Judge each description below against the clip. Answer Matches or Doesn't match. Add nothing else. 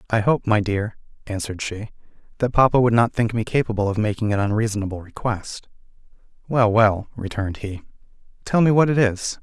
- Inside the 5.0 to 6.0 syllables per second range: Matches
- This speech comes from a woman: Doesn't match